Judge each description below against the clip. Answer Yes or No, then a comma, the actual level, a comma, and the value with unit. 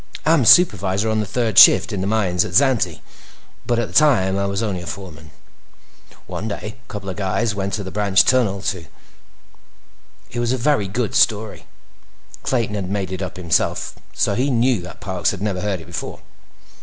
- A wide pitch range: No, average, 3.6 semitones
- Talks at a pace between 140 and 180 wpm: No, average, 195 wpm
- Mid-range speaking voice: No, low, 100 Hz